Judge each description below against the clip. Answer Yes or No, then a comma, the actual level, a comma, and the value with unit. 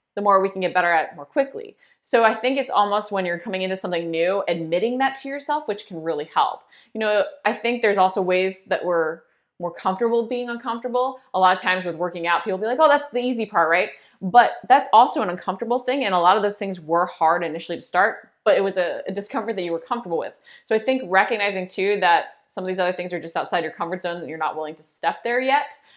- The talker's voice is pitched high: Yes, high, 195 Hz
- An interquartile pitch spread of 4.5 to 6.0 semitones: Yes, wide, 5.4 semitones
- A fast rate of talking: Yes, fast, 255 wpm